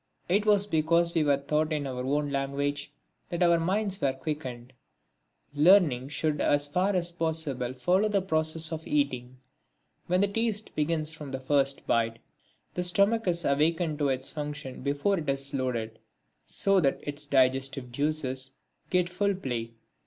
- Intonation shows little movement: No, average, 4.3 semitones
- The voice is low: No, medium, 150 Hz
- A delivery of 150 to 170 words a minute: Yes, average, 155 wpm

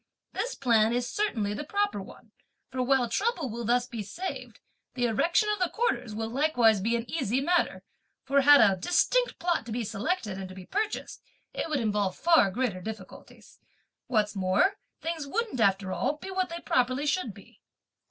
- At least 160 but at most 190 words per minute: Yes, average, 180 wpm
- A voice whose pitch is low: No, very high, 250 Hz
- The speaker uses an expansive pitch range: Yes, wide, 7.8 semitones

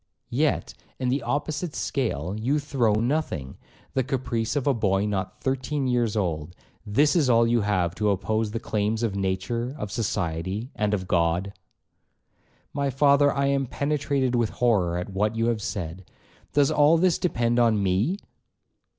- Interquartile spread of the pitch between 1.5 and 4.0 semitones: No, wide, 5.6 semitones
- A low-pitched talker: Yes, low, 115 Hz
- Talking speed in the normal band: Yes, average, 155 wpm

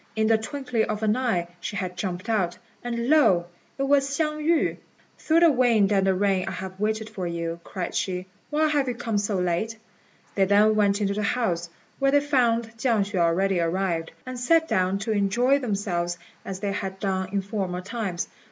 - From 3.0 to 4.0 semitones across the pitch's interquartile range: No, average, 4.5 semitones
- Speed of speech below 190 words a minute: No, average, 200 wpm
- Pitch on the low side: No, high, 205 Hz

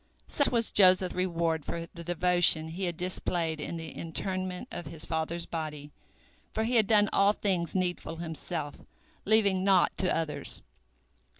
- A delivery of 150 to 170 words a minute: Yes, average, 155 wpm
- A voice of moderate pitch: Yes, medium, 175 Hz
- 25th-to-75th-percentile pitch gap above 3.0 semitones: No, narrow, 2.6 semitones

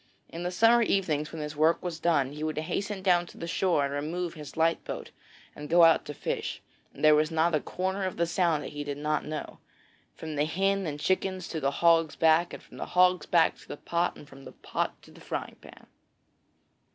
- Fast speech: Yes, fast, 225 wpm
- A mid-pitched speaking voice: Yes, medium, 165 Hz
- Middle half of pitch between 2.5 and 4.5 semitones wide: Yes, average, 2.9 semitones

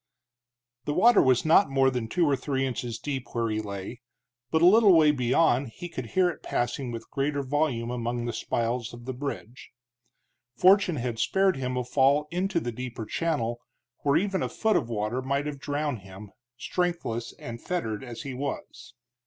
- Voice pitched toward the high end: No, low, 130 Hz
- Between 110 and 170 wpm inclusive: No, average, 185 wpm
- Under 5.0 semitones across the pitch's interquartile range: Yes, average, 4.5 semitones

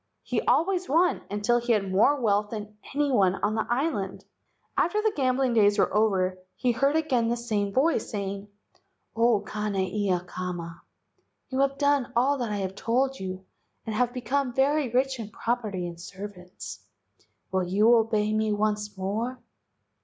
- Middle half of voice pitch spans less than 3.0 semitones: No, average, 4.6 semitones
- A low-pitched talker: No, high, 220 Hz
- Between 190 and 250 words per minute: No, average, 160 wpm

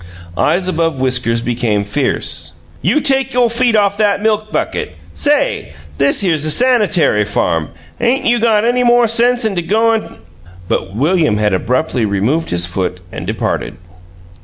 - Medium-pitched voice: Yes, medium, 175 Hz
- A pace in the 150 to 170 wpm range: Yes, average, 160 wpm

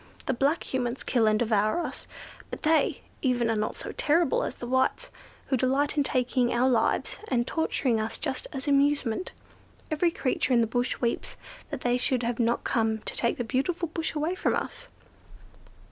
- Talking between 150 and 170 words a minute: No, average, 185 wpm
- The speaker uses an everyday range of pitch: Yes, average, 3.5 semitones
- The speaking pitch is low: No, very high, 255 Hz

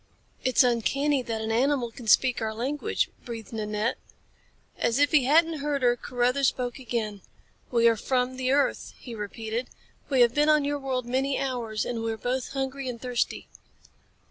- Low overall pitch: No, very high, 250 Hz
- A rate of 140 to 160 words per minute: No, average, 175 wpm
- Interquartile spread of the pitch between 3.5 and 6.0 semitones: No, average, 2.9 semitones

